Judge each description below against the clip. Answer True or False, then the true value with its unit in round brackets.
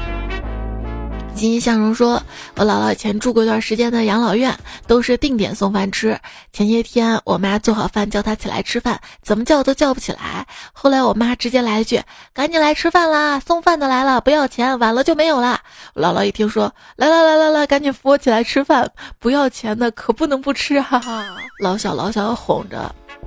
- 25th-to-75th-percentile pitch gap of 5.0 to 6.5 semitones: False (4.3 semitones)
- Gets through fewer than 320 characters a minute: True (290 characters per minute)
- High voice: True (235 Hz)